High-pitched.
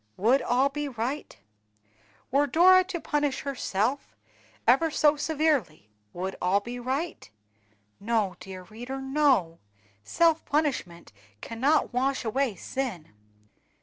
Yes: very high, 260 Hz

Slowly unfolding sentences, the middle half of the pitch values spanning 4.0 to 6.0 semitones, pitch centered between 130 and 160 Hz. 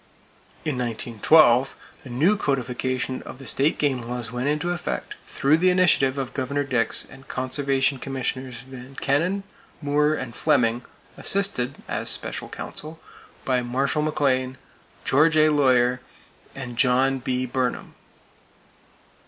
No: slow, 130 wpm; average, 2.9 semitones; low, 135 Hz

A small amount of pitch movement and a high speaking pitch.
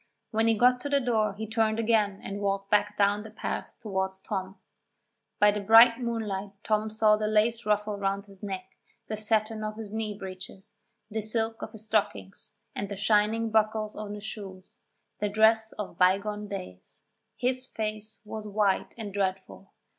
Yes: narrow, 1.7 semitones; high, 210 Hz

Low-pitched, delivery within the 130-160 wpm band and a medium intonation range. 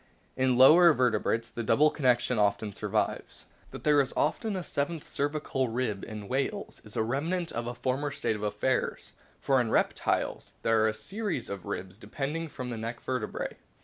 No: low, 125 Hz; average, 180 wpm; average, 4.7 semitones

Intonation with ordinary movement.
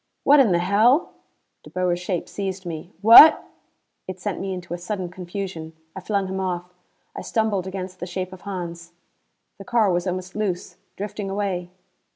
No: narrow, 2.1 semitones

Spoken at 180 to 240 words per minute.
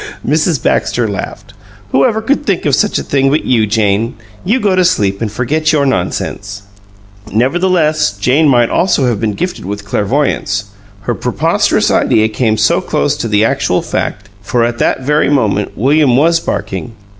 No: average, 170 wpm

